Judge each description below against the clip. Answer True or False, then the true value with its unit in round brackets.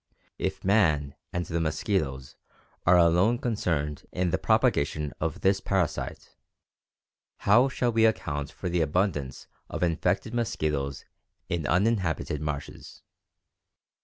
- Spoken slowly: True (115 wpm)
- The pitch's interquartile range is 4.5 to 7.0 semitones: True (4.9 semitones)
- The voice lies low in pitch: True (85 Hz)